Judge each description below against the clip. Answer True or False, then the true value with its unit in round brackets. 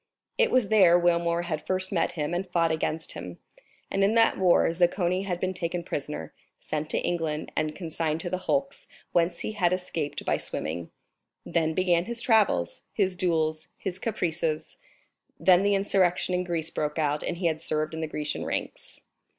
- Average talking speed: True (180 wpm)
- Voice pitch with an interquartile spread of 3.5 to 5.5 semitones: False (2.9 semitones)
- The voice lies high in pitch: False (175 Hz)